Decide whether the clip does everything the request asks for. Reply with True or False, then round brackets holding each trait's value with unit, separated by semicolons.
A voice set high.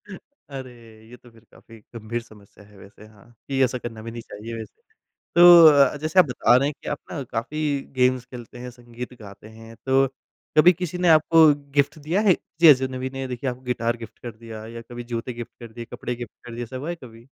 False (125 Hz)